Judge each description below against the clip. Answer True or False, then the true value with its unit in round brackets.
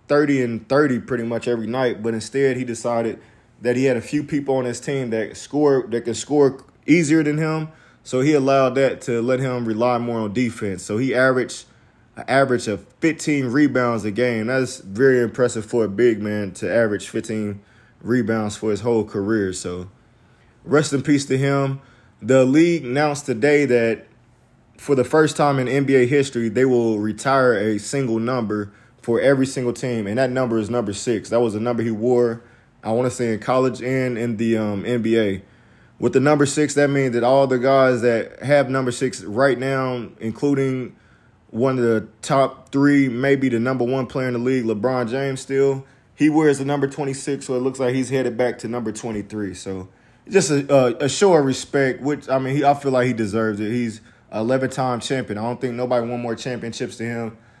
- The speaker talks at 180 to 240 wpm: True (200 wpm)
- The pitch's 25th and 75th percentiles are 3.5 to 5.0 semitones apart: False (2.9 semitones)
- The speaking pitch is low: True (125 Hz)